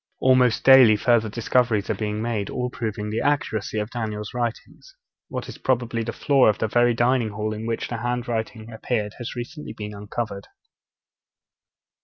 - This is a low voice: Yes, low, 115 Hz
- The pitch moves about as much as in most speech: No, narrow, 2.3 semitones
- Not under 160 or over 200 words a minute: Yes, average, 170 wpm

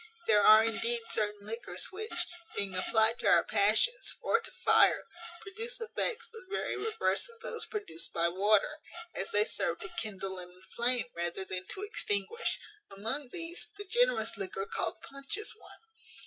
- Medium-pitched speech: No, high, 225 Hz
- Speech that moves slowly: No, average, 160 wpm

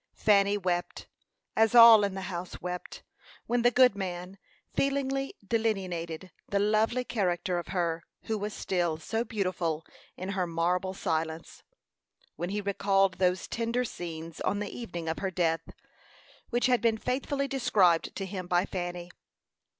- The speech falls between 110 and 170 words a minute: Yes, average, 150 wpm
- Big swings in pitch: No, average, 4.1 semitones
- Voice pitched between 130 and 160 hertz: No, high, 190 Hz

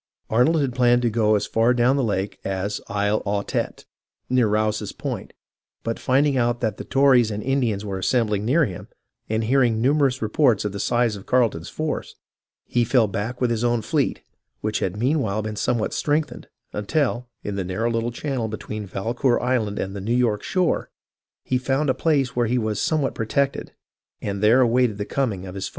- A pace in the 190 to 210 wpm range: Yes, average, 195 wpm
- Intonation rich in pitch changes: No, average, 3.4 semitones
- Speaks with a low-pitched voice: Yes, low, 115 Hz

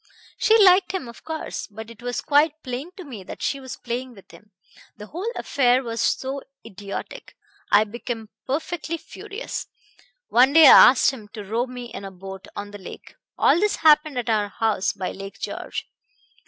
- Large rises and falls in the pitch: Yes, wide, 6.2 semitones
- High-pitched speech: Yes, high, 245 Hz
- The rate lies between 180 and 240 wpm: Yes, average, 185 wpm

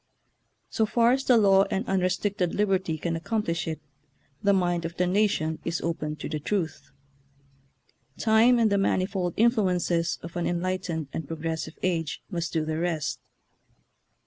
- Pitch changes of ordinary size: Yes, average, 3.5 semitones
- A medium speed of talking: Yes, average, 155 wpm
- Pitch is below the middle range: No, medium, 180 Hz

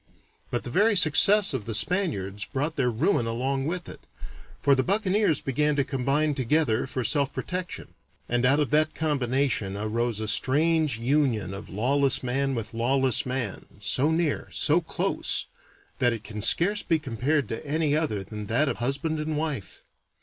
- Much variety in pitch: No, average, 4.9 semitones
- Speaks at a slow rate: No, average, 170 wpm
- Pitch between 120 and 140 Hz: Yes, low, 135 Hz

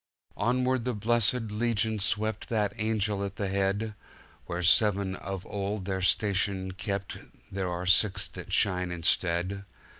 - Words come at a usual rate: No, slow, 130 wpm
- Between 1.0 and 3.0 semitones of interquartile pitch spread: Yes, narrow, 2.4 semitones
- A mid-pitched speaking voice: No, low, 100 Hz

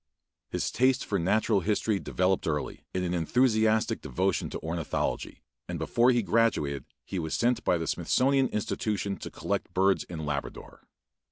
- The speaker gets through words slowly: No, average, 155 wpm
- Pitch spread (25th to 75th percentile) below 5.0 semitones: No, average, 5.3 semitones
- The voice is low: Yes, low, 100 Hz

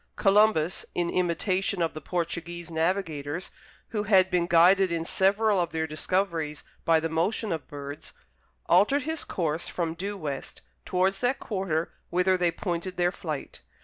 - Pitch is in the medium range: Yes, medium, 175 Hz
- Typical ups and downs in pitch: Yes, average, 3.1 semitones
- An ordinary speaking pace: Yes, average, 150 wpm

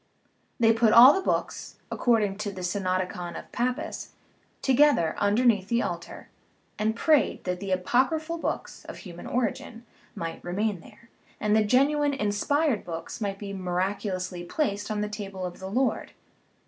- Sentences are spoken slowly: No, average, 160 wpm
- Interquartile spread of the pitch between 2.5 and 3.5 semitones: No, average, 4.8 semitones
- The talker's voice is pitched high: Yes, high, 210 Hz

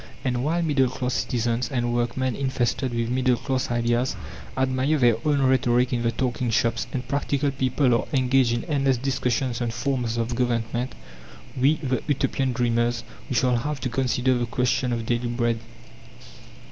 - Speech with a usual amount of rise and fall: No, narrow, 1.9 semitones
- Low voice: Yes, low, 125 Hz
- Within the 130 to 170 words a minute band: Yes, average, 165 wpm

